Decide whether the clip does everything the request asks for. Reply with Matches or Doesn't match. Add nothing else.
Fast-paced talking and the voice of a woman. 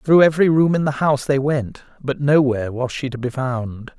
Doesn't match